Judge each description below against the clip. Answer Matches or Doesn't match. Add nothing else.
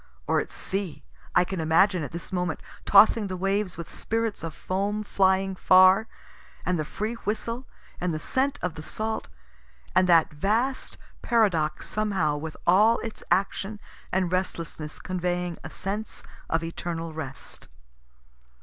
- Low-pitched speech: Doesn't match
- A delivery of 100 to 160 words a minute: Matches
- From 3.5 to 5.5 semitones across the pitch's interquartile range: Matches